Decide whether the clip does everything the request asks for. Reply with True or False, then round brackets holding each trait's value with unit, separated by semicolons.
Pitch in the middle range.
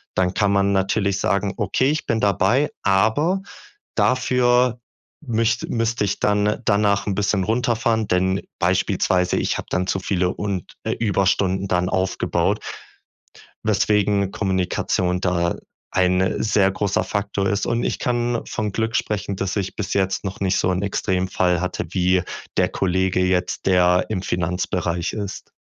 False (100 Hz)